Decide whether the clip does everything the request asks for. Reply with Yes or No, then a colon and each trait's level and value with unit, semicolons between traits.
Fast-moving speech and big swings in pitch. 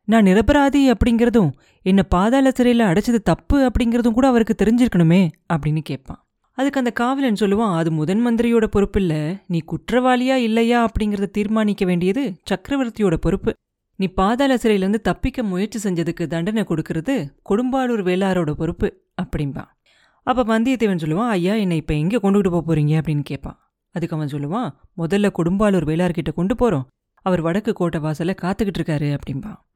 Yes: fast, 140 wpm; wide, 5.7 semitones